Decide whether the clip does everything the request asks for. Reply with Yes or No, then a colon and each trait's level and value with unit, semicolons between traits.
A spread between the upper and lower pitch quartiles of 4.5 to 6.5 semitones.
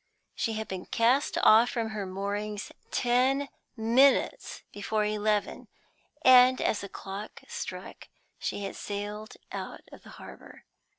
No: average, 3.3 semitones